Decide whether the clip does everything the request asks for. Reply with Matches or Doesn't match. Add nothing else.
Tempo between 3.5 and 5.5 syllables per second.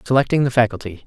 Doesn't match